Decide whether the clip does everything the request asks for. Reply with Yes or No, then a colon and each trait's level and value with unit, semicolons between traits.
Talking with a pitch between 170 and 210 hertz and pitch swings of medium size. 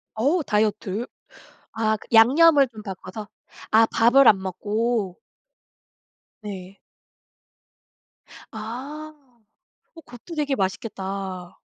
No: high, 220 Hz; average, 4.5 semitones